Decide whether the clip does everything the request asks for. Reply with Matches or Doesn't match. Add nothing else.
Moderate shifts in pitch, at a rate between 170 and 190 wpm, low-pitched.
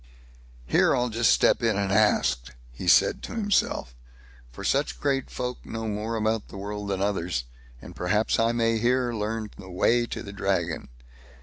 Matches